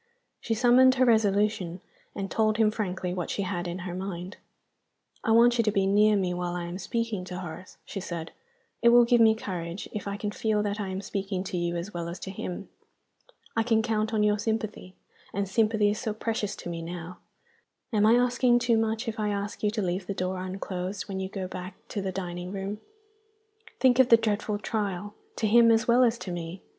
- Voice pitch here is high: Yes, high, 205 Hz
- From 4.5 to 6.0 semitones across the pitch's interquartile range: No, average, 3.4 semitones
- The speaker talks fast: Yes, fast, 215 wpm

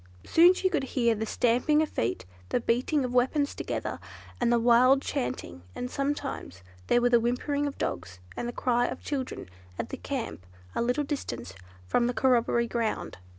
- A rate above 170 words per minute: Yes, average, 180 wpm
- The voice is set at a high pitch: Yes, high, 245 Hz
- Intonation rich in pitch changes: No, average, 3.0 semitones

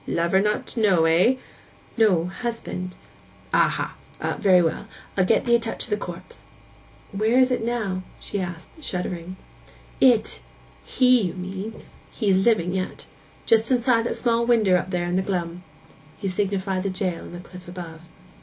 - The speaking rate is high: No, average, 160 wpm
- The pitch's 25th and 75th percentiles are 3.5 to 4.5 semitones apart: Yes, average, 4.0 semitones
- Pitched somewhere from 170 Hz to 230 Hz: Yes, high, 190 Hz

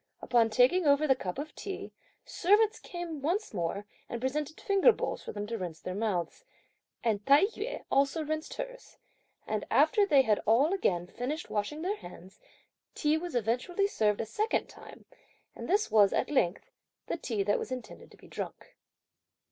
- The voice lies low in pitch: No, very high, 275 Hz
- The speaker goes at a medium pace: Yes, average, 175 wpm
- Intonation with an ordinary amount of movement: No, wide, 8.7 semitones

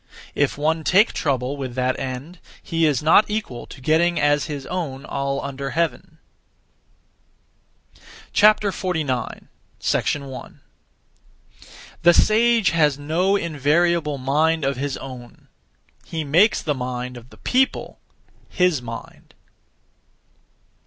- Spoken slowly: Yes, slow, 110 wpm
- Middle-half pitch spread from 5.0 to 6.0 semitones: No, average, 4.3 semitones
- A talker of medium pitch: Yes, medium, 150 Hz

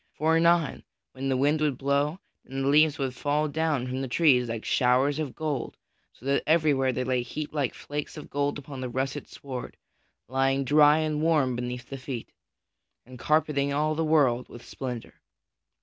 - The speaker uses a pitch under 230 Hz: Yes, medium, 140 Hz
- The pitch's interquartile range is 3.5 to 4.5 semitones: No, average, 2.9 semitones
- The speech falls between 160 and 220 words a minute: Yes, average, 180 wpm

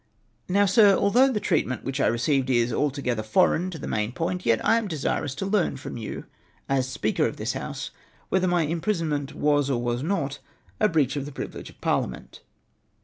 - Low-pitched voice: No, medium, 145 Hz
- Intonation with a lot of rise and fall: Yes, wide, 6.0 semitones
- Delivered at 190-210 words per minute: Yes, fast, 205 wpm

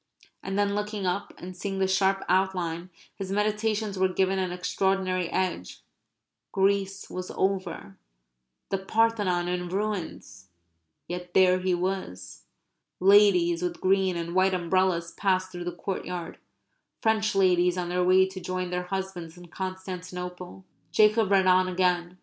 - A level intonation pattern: Yes, narrow, 1.4 semitones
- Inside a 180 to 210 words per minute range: No, average, 140 wpm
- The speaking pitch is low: No, medium, 185 Hz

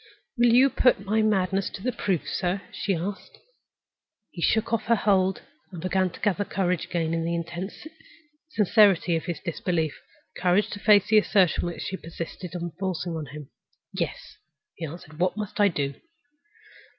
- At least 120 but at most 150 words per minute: No, average, 170 wpm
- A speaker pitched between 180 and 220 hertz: Yes, medium, 185 Hz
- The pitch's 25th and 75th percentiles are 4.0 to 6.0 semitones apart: No, average, 3.3 semitones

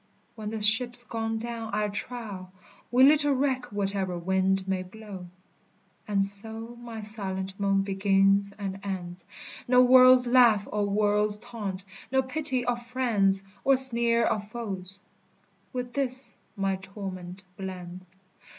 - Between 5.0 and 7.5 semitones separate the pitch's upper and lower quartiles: No, average, 3.8 semitones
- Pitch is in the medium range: No, high, 210 Hz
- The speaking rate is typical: No, slow, 130 wpm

